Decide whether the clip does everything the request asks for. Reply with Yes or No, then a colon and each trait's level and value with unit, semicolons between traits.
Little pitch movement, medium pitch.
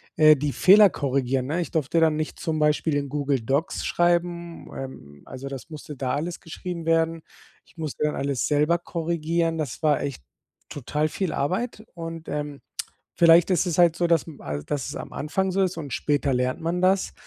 No: average, 3.2 semitones; medium, 155 Hz